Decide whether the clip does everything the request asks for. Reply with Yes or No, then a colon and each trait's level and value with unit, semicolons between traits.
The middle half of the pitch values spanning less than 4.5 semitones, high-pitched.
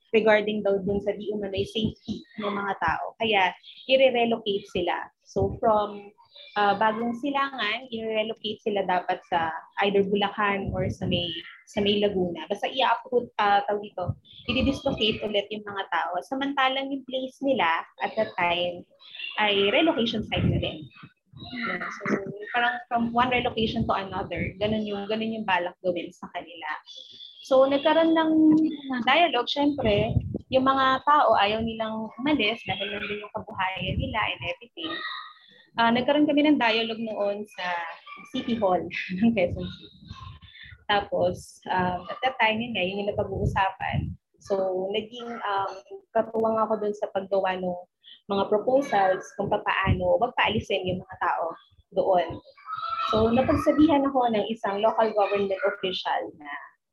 Yes: average, 4.0 semitones; high, 215 Hz